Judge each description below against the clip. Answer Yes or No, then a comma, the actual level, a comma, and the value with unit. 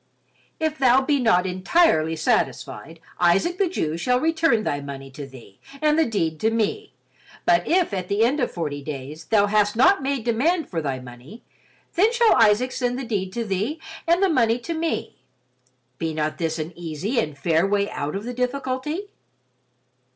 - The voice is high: Yes, high, 220 Hz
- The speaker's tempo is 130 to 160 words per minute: No, average, 180 wpm